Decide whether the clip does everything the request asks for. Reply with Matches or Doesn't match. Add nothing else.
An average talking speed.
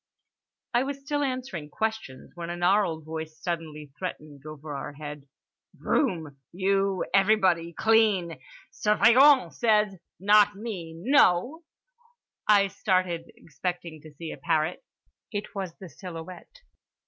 Doesn't match